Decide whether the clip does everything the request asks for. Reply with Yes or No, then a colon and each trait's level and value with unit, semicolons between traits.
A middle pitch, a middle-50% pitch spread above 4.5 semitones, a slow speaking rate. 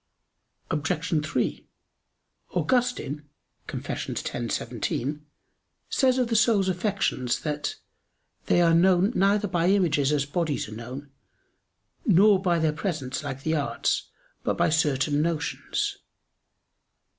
Yes: medium, 165 Hz; average, 5.0 semitones; slow, 115 wpm